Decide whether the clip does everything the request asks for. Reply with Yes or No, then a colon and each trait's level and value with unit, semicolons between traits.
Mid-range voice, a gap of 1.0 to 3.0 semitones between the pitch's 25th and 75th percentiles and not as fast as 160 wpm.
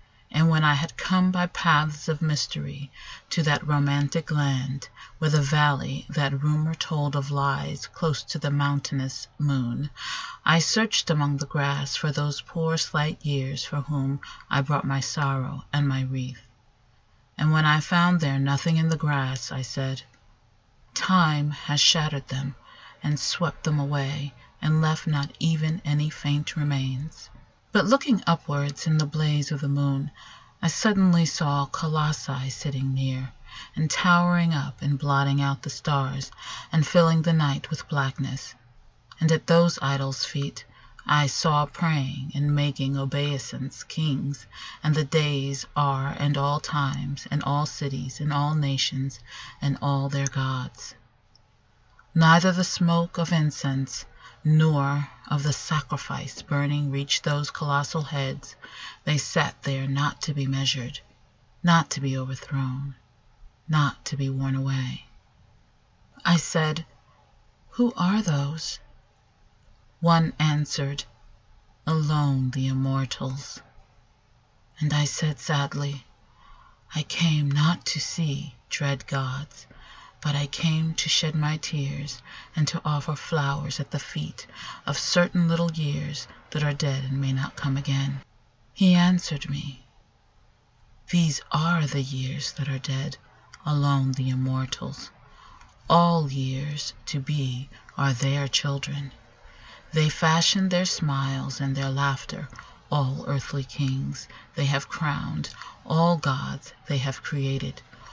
Yes: medium, 145 Hz; narrow, 2.4 semitones; slow, 135 wpm